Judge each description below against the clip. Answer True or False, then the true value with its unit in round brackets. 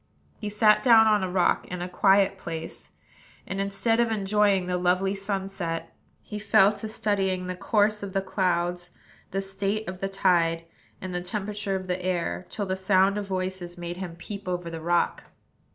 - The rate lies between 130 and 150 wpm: False (185 wpm)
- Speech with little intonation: True (2.1 semitones)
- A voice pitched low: False (190 Hz)